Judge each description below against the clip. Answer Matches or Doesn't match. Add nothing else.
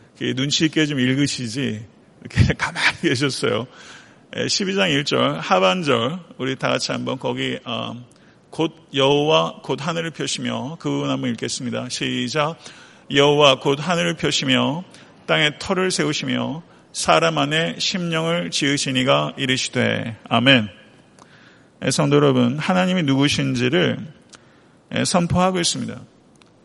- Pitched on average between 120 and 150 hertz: Matches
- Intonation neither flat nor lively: Matches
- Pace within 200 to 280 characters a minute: Matches